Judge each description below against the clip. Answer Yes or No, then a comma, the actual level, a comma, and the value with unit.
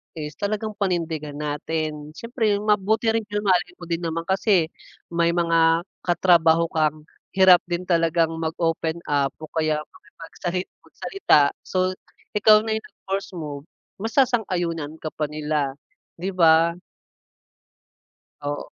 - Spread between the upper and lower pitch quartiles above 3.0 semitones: Yes, average, 3.4 semitones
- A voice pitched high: No, medium, 170 Hz